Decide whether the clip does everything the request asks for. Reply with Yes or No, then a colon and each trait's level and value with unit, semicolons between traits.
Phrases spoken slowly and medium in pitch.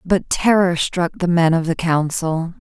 No: average, 180 wpm; medium, 170 Hz